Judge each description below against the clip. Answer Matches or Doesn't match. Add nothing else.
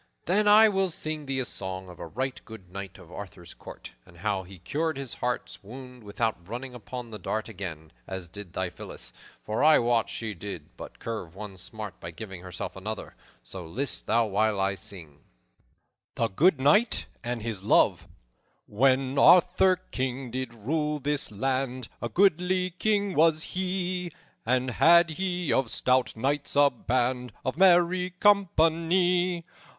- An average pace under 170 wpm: Matches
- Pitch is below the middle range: Matches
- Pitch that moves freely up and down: Matches